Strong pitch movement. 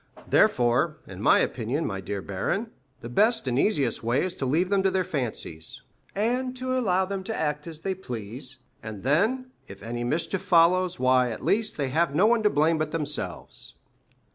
Yes: wide, 7.8 semitones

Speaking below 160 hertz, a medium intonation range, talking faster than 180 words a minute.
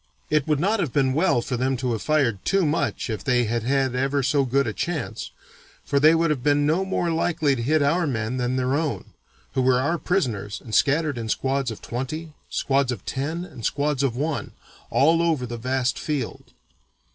Yes: medium, 140 Hz; average, 3.6 semitones; fast, 205 wpm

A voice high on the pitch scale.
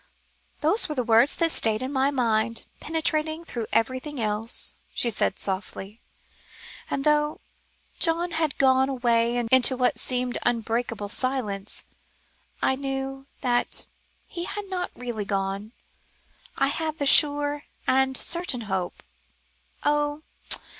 Yes: very high, 260 Hz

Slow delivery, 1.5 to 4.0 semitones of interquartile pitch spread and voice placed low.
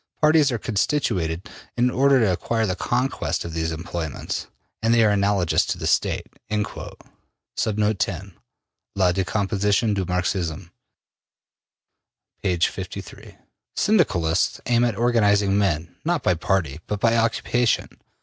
No: slow, 120 wpm; average, 5.0 semitones; low, 100 Hz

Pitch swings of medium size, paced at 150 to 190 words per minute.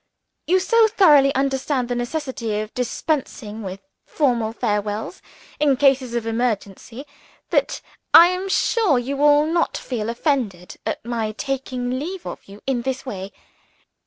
No: average, 4.5 semitones; average, 140 wpm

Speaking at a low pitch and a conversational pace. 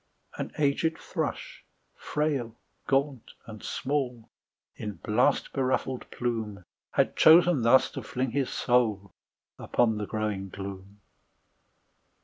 No: low, 120 Hz; slow, 110 wpm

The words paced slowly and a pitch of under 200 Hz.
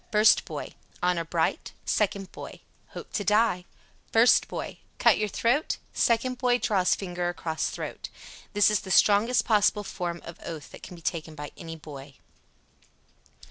No: average, 155 wpm; high, 190 Hz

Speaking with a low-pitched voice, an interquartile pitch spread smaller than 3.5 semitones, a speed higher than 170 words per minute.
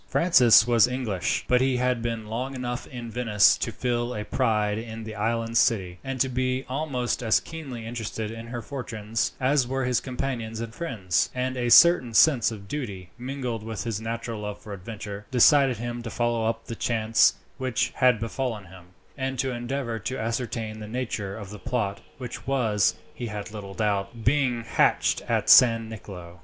Yes: low, 115 Hz; average, 2.7 semitones; average, 180 wpm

